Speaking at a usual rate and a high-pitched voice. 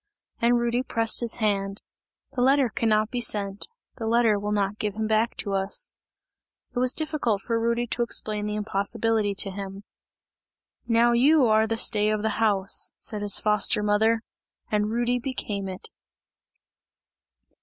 Yes: average, 155 wpm; high, 220 Hz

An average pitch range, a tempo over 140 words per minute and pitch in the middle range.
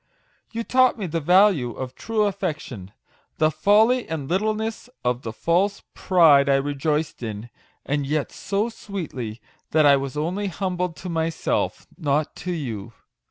No: wide, 6.2 semitones; average, 150 wpm; medium, 160 Hz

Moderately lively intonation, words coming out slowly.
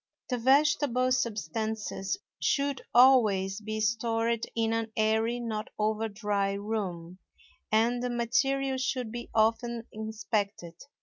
No: narrow, 2.3 semitones; slow, 115 wpm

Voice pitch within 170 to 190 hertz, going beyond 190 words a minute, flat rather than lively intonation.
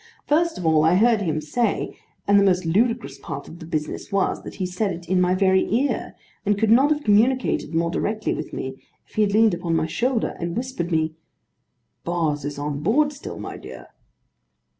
No: medium, 185 Hz; fast, 205 wpm; wide, 5.6 semitones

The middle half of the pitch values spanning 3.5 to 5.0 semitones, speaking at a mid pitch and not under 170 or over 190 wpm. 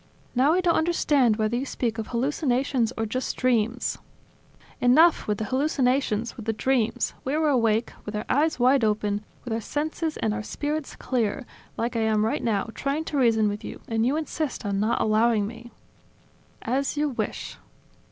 No: average, 4.1 semitones; high, 240 Hz; average, 180 wpm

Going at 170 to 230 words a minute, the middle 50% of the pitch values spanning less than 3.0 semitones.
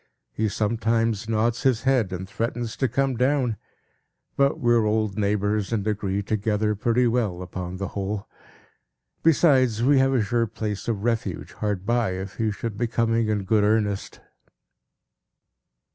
No: average, 155 wpm; narrow, 2.6 semitones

